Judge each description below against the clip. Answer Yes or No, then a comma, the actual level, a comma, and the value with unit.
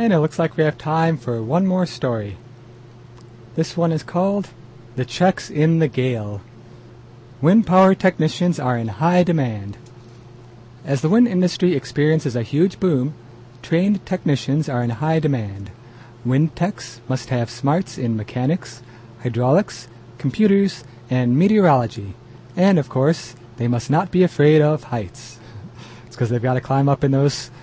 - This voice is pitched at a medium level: No, low, 130 Hz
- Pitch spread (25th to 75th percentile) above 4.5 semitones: Yes, average, 5.3 semitones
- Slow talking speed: No, average, 155 wpm